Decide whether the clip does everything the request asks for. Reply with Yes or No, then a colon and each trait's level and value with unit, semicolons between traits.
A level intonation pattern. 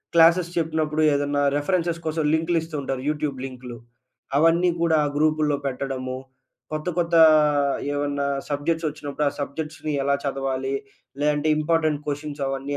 Yes: narrow, 2.3 semitones